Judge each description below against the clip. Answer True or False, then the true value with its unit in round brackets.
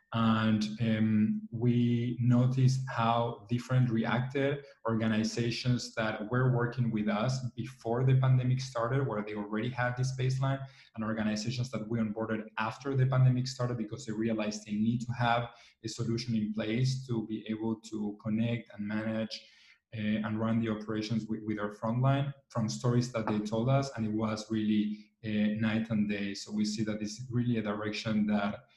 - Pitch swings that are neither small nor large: False (2.1 semitones)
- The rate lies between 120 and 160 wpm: False (175 wpm)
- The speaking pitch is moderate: False (115 Hz)